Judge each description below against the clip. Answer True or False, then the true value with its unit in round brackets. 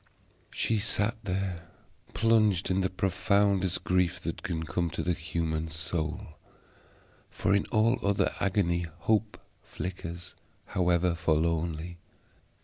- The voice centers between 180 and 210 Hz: False (90 Hz)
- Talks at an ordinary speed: False (115 wpm)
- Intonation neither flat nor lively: True (3.0 semitones)